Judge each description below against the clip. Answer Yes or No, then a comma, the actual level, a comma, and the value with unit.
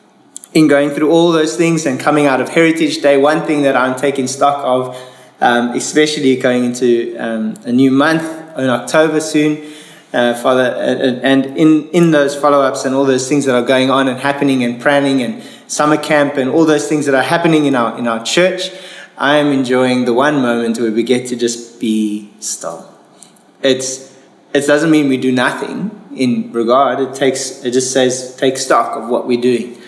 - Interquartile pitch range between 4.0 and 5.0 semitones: No, average, 3.2 semitones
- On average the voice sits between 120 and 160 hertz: Yes, low, 135 Hz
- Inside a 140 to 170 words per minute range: No, average, 195 wpm